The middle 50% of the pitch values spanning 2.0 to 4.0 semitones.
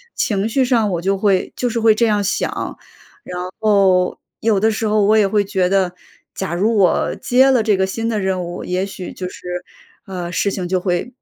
Yes: average, 3.1 semitones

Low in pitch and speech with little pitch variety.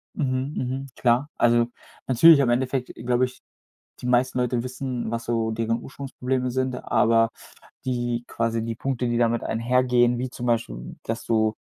Yes: low, 120 Hz; narrow, 1.8 semitones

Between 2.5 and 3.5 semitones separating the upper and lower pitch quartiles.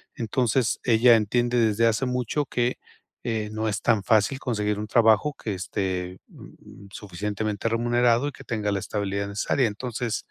Yes: average, 2.8 semitones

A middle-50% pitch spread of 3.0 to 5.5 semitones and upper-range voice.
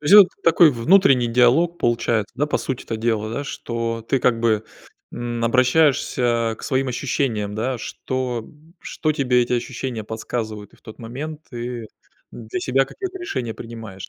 No: average, 3.4 semitones; low, 120 Hz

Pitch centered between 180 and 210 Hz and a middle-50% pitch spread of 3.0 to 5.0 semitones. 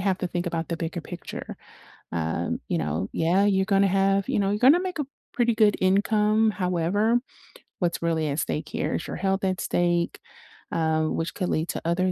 Yes: medium, 185 Hz; average, 3.4 semitones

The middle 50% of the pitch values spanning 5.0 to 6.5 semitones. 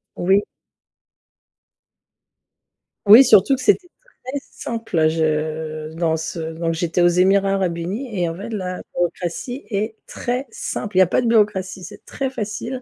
Yes: wide, 5.5 semitones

